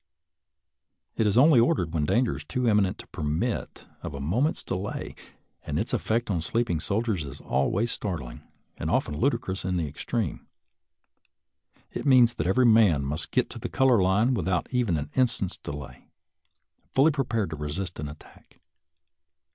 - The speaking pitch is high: No, very low, 95 Hz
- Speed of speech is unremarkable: Yes, average, 165 wpm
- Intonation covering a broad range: Yes, wide, 7.0 semitones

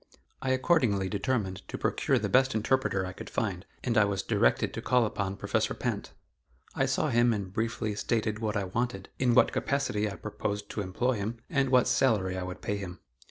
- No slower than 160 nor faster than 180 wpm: No, average, 200 wpm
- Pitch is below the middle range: Yes, low, 105 Hz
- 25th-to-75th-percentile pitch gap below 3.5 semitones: No, average, 3.9 semitones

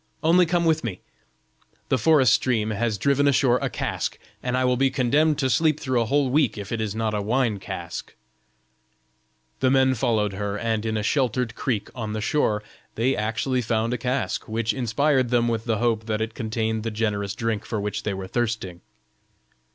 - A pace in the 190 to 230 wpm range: Yes, average, 195 wpm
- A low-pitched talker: Yes, low, 115 Hz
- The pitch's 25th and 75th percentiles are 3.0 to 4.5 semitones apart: Yes, average, 3.3 semitones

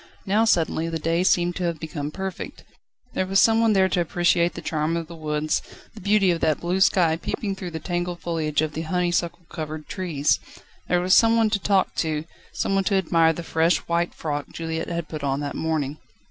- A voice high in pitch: No, medium, 170 Hz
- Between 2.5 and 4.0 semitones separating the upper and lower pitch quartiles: Yes, average, 2.9 semitones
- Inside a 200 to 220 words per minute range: Yes, fast, 205 wpm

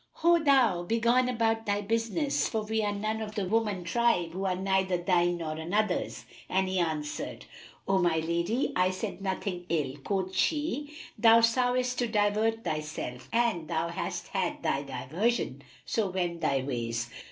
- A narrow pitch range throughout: No, average, 4.9 semitones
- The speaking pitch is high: Yes, high, 195 Hz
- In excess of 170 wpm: No, average, 165 wpm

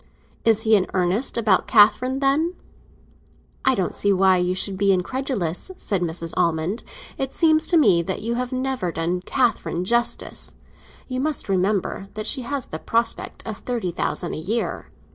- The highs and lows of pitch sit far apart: Yes, wide, 5.8 semitones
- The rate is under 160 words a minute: No, average, 165 wpm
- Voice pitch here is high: Yes, high, 210 Hz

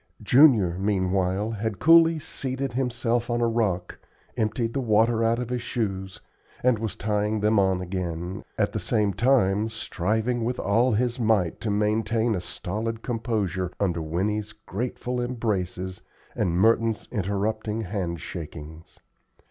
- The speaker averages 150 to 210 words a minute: No, average, 140 wpm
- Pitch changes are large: No, average, 3.6 semitones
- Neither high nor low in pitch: No, low, 110 Hz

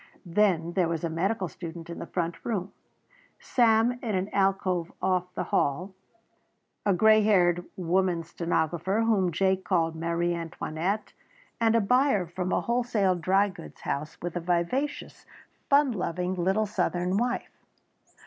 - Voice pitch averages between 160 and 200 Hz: Yes, medium, 185 Hz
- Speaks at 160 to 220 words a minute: No, average, 145 wpm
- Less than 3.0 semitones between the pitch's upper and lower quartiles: No, average, 3.6 semitones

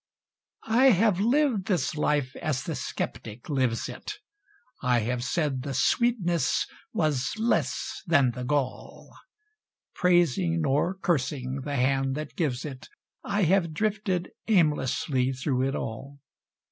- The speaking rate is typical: No, slow, 125 wpm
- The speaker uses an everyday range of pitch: No, wide, 5.7 semitones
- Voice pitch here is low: No, medium, 150 Hz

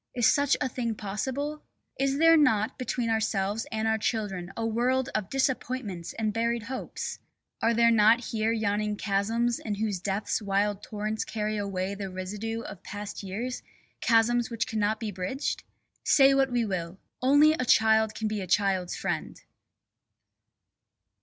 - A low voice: No, high, 220 Hz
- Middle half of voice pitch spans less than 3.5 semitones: Yes, average, 2.9 semitones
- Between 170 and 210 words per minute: No, average, 155 wpm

